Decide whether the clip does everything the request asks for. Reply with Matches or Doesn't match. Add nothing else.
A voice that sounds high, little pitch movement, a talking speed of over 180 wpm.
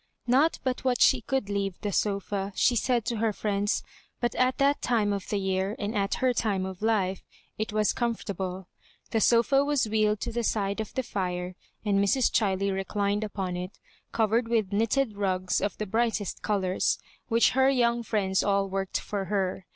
Doesn't match